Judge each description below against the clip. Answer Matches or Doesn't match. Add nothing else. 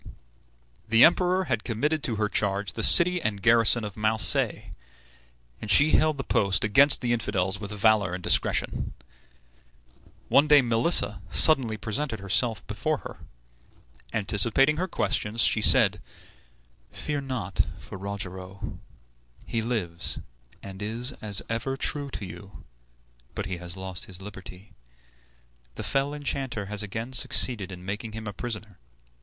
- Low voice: Matches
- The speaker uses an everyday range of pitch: Matches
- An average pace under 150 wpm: Matches